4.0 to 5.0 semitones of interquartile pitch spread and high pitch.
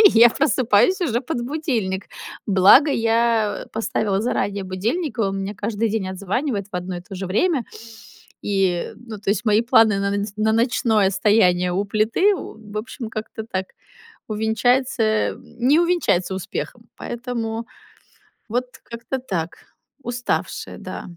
No: average, 3.6 semitones; high, 220 Hz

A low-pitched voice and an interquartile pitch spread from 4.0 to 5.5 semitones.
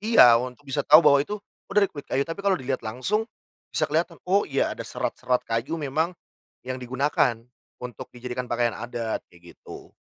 Yes: low, 130 Hz; average, 4.6 semitones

